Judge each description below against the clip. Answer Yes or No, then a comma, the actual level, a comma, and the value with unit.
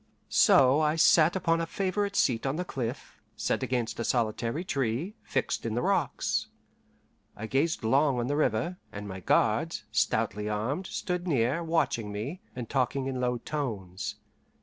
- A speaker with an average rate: Yes, average, 160 wpm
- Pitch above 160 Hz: No, low, 130 Hz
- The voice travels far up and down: Yes, wide, 6.1 semitones